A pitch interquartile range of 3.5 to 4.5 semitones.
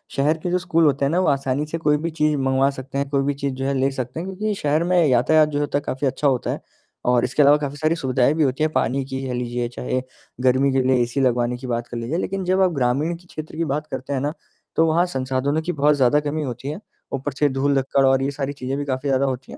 No: narrow, 2.6 semitones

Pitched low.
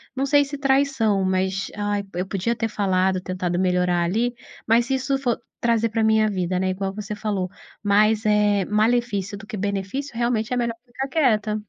No: high, 210 Hz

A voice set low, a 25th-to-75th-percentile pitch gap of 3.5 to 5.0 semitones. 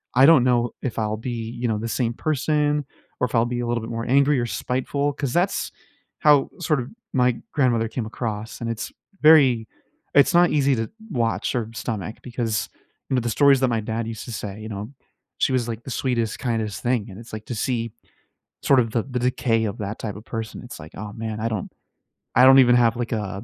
No: low, 120 Hz; average, 2.7 semitones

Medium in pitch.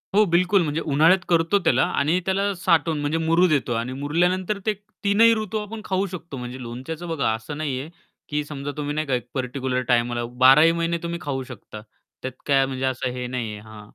Yes: medium, 150 Hz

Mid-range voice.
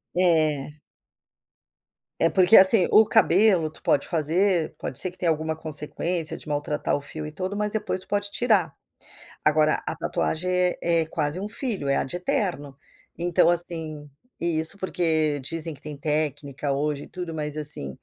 Yes: medium, 160 Hz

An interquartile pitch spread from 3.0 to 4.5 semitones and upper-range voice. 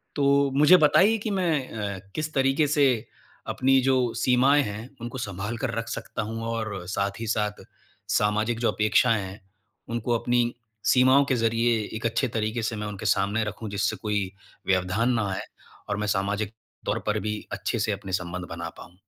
No: average, 3.9 semitones; low, 115 Hz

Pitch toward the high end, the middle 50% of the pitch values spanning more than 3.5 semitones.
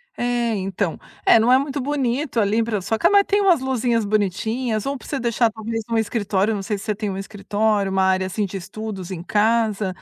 No: high, 220 Hz; average, 3.1 semitones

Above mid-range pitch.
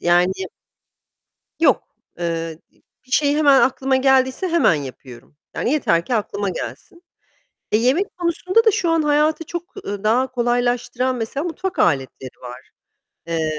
Yes: very high, 255 Hz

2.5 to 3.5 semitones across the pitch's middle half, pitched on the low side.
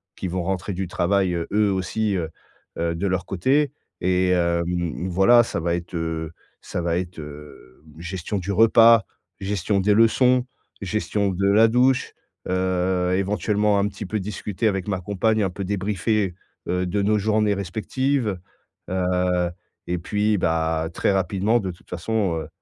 Yes: average, 3.0 semitones; very low, 95 Hz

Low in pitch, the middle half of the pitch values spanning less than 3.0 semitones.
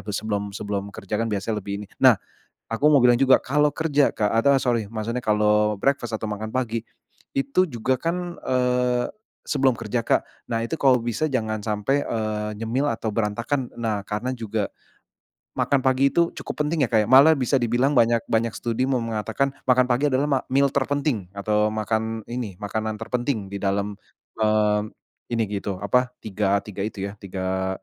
No: low, 115 Hz; average, 3.7 semitones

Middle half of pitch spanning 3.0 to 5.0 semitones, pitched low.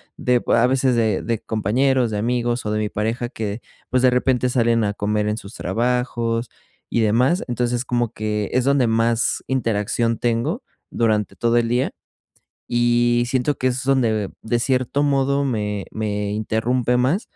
No: narrow, 2.5 semitones; low, 120 Hz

